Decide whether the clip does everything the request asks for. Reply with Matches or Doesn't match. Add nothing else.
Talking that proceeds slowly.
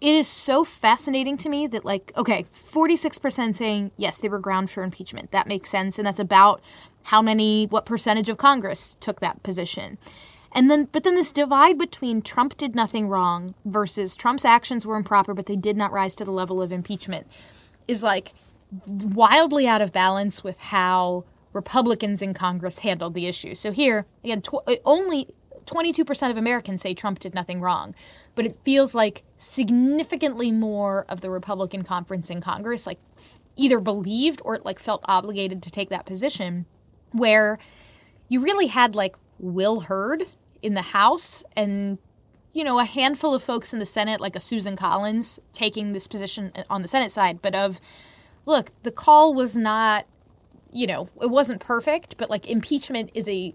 Doesn't match